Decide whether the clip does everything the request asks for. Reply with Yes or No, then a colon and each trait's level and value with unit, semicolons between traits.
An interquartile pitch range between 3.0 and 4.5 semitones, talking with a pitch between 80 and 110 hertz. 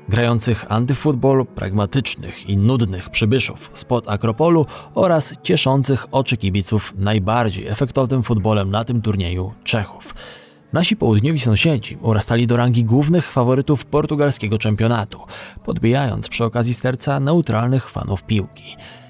No: average, 4.1 semitones; low, 120 Hz